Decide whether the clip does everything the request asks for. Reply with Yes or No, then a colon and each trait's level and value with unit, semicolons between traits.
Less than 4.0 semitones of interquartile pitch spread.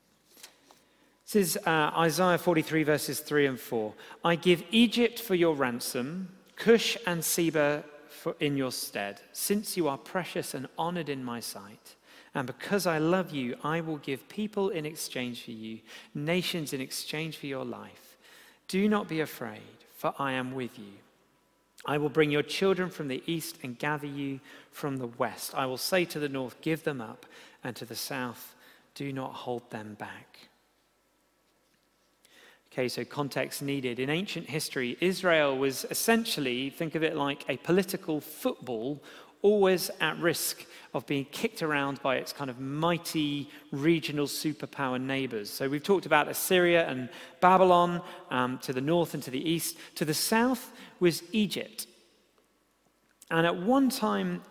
No: average, 4.6 semitones